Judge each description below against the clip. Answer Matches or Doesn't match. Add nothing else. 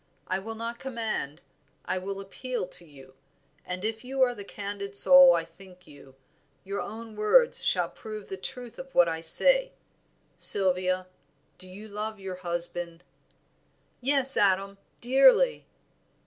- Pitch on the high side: Matches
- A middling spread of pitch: Matches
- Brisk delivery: Doesn't match